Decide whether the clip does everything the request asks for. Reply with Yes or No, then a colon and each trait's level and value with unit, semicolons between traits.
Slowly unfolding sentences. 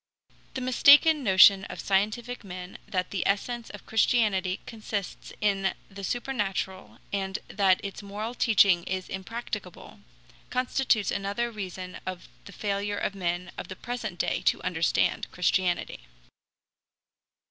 Yes: slow, 125 wpm